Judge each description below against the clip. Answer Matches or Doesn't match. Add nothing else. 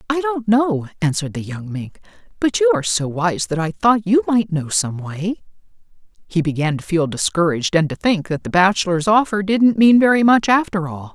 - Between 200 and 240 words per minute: Matches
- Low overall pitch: Doesn't match